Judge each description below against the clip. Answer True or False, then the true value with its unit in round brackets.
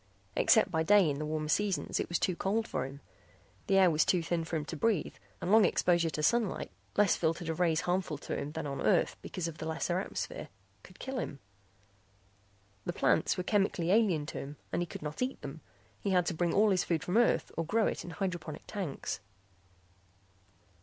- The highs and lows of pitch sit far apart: False (3.8 semitones)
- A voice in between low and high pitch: True (175 Hz)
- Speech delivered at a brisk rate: True (210 wpm)